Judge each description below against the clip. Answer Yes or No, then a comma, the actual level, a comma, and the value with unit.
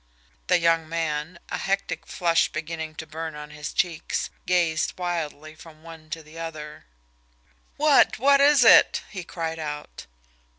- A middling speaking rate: Yes, average, 145 wpm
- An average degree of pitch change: No, narrow, 2.1 semitones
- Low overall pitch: No, medium, 165 Hz